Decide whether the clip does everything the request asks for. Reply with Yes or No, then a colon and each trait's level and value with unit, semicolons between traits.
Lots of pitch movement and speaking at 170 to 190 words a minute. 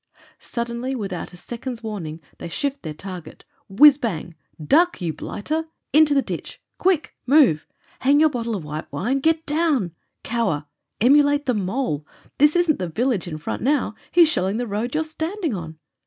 Yes: wide, 8.3 semitones; average, 180 wpm